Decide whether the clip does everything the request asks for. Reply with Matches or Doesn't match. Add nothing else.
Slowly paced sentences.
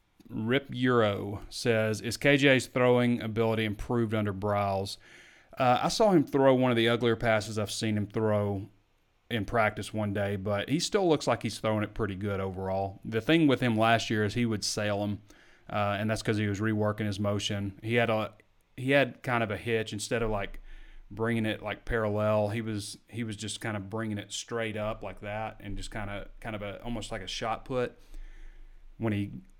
Doesn't match